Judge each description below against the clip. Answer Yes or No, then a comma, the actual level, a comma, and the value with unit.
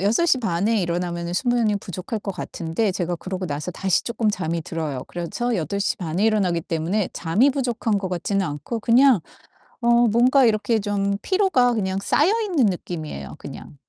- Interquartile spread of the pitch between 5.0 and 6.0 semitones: Yes, wide, 5.4 semitones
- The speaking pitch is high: Yes, high, 200 Hz